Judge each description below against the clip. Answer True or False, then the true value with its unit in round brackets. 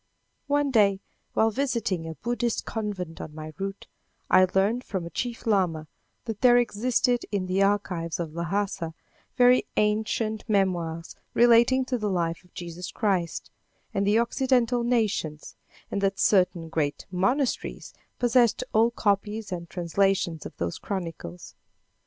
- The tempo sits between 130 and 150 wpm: True (140 wpm)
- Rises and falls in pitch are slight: False (5.3 semitones)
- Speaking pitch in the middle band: False (200 Hz)